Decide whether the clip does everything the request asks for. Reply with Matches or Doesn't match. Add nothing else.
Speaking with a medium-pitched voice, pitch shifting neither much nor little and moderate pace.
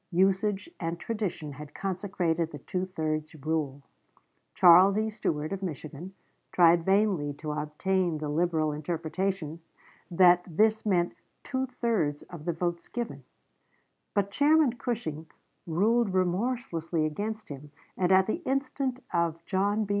Doesn't match